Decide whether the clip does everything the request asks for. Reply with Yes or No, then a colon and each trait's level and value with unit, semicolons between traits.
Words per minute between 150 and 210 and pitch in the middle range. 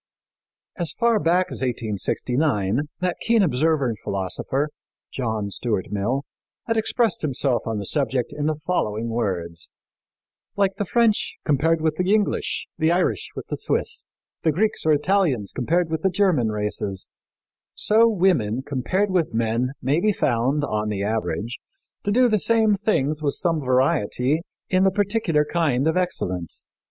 Yes: average, 155 wpm; medium, 150 Hz